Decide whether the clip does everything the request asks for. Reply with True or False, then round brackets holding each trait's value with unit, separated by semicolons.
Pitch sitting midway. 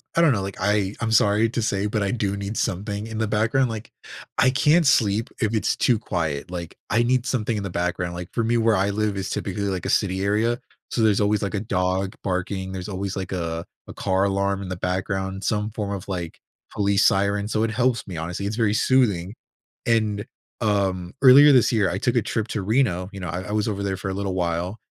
False (100 Hz)